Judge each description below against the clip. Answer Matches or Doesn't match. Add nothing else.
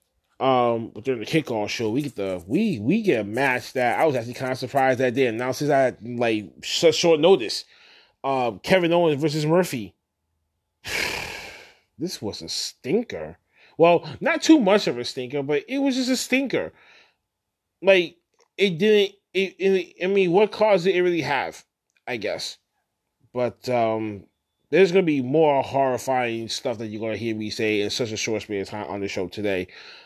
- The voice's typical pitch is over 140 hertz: Doesn't match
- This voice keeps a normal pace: Matches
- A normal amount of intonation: Doesn't match